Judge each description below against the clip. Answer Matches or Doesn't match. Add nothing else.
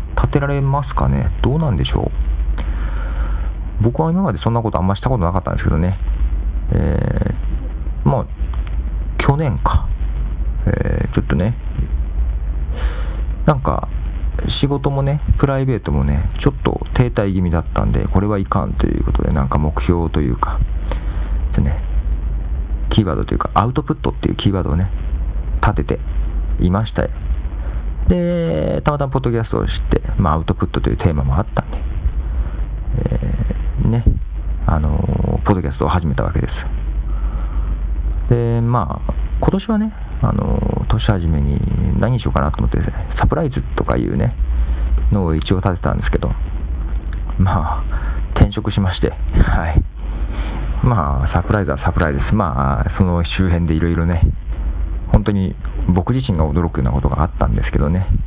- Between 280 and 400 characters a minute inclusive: Matches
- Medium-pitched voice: Doesn't match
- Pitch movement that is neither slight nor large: Doesn't match